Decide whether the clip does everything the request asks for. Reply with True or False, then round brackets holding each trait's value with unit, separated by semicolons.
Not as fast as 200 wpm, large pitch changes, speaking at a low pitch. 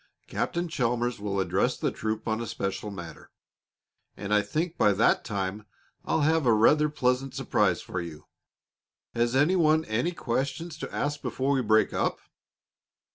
True (160 wpm; 5.8 semitones; 120 Hz)